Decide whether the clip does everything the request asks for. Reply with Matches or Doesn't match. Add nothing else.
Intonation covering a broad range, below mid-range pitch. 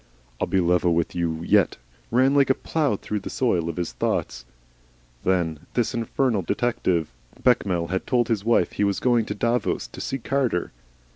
Matches